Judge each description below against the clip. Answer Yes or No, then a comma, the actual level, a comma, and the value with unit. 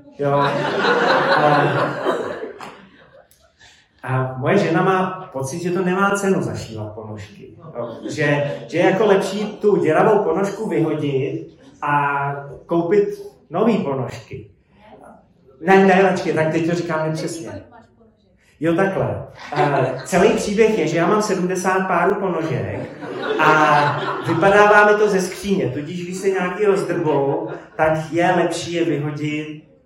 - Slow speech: No, average, 125 wpm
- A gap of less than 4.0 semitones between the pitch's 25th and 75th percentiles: No, average, 4.9 semitones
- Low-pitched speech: No, medium, 165 Hz